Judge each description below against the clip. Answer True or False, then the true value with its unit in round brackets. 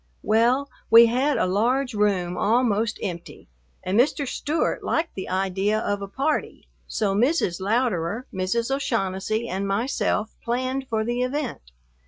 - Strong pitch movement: False (4.5 semitones)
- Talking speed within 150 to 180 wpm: False (140 wpm)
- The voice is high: True (225 Hz)